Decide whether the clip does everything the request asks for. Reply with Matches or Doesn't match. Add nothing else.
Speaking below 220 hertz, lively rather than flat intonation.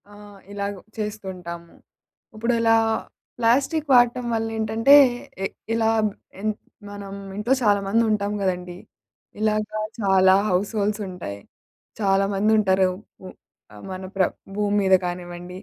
Doesn't match